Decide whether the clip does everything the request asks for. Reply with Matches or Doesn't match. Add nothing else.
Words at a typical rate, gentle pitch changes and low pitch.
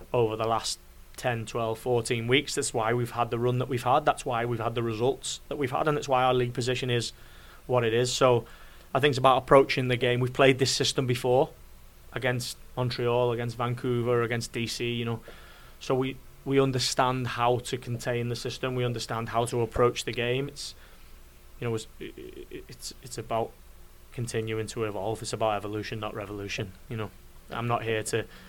Matches